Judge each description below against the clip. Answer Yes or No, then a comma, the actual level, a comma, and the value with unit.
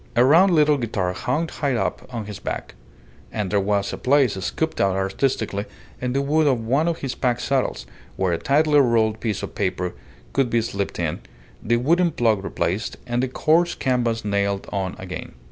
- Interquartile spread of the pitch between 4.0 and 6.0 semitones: Yes, wide, 5.6 semitones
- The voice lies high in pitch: No, low, 120 Hz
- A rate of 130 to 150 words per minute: No, average, 190 wpm